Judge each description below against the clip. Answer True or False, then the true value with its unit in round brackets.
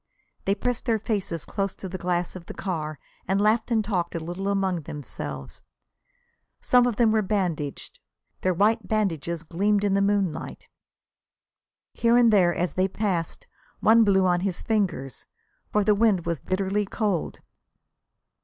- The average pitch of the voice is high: True (195 Hz)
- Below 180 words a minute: True (155 wpm)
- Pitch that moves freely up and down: False (3.4 semitones)